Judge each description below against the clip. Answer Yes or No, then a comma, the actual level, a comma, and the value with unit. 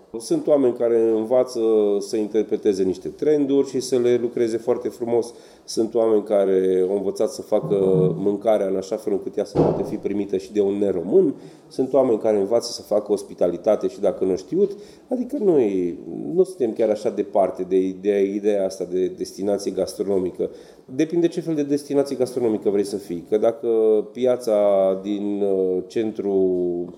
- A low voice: Yes, low, 110 Hz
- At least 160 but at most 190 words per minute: Yes, average, 165 wpm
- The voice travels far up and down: Yes, wide, 5.8 semitones